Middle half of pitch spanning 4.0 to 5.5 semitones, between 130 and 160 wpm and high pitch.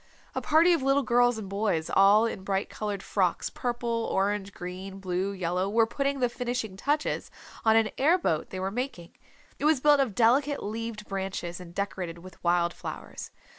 No: average, 4.6 semitones; average, 180 wpm; high, 210 Hz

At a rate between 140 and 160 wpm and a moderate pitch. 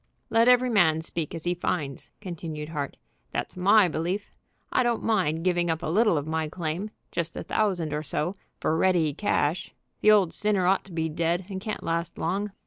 No: average, 195 wpm; medium, 175 Hz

